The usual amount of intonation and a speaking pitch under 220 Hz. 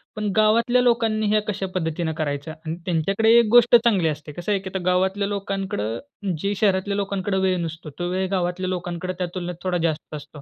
Yes: average, 3.3 semitones; high, 190 Hz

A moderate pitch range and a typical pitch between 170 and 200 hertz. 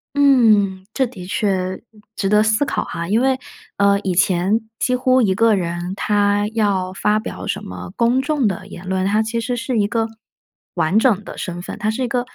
No: average, 3.8 semitones; high, 210 Hz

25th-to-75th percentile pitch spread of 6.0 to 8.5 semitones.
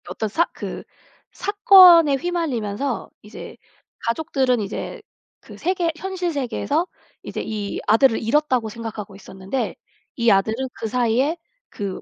Yes: wide, 7.0 semitones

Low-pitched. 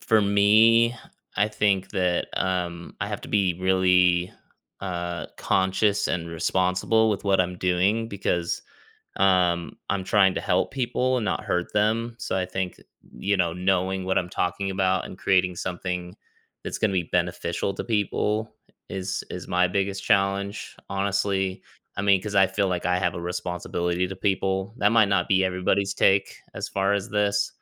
Yes: very low, 95 Hz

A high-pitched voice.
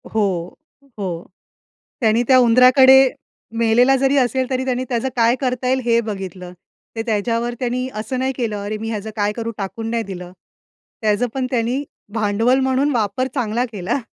Yes: high, 235 Hz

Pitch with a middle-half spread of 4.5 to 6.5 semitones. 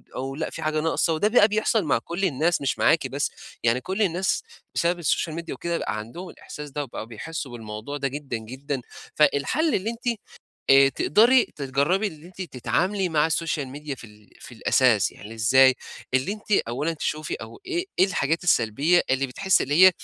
Yes: wide, 5.4 semitones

